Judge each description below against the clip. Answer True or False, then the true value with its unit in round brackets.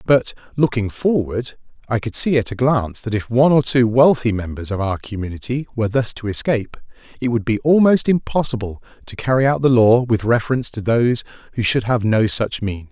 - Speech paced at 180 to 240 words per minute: True (200 wpm)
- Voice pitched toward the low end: True (120 Hz)